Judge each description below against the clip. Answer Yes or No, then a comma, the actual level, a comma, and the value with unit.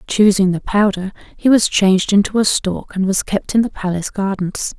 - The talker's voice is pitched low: No, high, 195 Hz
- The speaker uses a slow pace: No, average, 200 wpm